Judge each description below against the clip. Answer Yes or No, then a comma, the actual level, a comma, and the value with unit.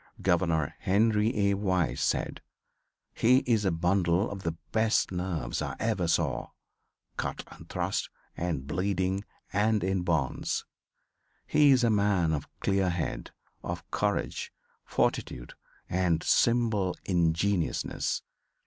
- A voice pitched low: Yes, very low, 95 Hz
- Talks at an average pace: No, slow, 120 wpm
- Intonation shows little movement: No, average, 3.6 semitones